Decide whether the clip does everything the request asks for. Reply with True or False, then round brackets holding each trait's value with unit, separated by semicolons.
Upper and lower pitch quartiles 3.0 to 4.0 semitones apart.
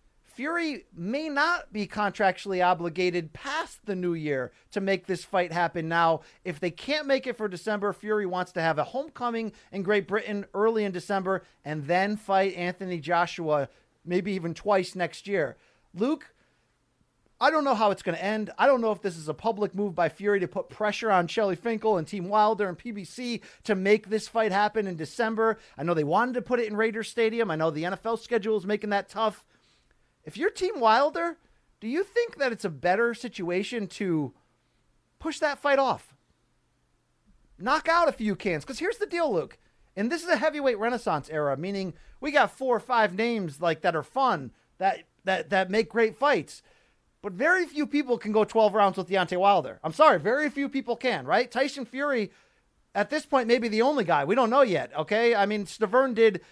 False (5.0 semitones)